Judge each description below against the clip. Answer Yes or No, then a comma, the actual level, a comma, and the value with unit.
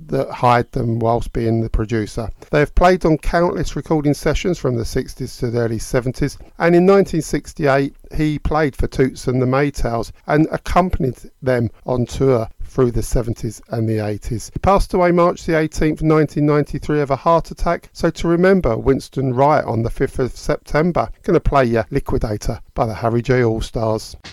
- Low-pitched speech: Yes, low, 130 Hz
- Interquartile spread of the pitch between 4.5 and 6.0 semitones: Yes, average, 5.0 semitones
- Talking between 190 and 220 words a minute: No, average, 180 wpm